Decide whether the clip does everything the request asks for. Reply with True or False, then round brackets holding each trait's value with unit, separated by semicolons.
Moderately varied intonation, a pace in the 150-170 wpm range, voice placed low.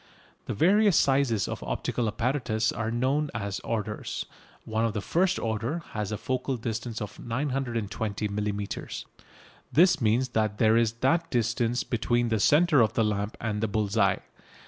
True (3.5 semitones; 160 wpm; 115 Hz)